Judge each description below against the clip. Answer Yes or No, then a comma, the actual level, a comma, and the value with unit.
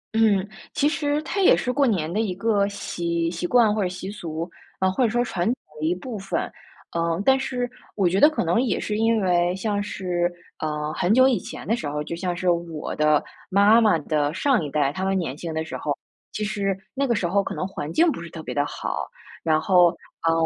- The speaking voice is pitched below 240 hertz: Yes, medium, 185 Hz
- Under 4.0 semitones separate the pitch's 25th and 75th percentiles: No, average, 5.0 semitones